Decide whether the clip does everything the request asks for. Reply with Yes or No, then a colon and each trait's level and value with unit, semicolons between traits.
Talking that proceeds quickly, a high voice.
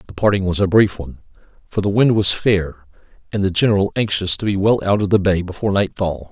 No: fast, 230 wpm; very low, 95 Hz